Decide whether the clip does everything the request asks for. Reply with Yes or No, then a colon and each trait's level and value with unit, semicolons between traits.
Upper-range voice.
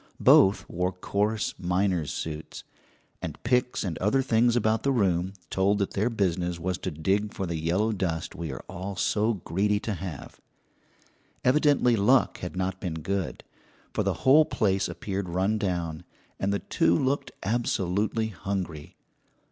No: very low, 95 Hz